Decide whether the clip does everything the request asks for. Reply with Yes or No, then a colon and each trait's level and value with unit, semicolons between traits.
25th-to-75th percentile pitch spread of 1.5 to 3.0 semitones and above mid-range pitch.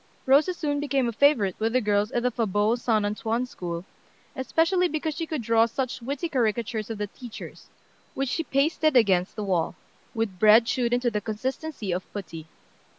No: average, 4.6 semitones; high, 235 Hz